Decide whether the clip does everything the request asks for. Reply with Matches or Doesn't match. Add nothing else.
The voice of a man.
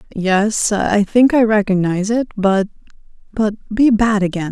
Doesn't match